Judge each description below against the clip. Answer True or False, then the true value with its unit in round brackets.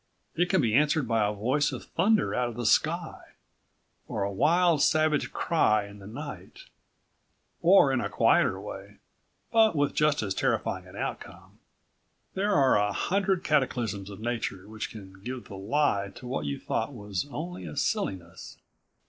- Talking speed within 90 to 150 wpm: False (165 wpm)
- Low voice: True (120 Hz)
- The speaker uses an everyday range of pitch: False (6.9 semitones)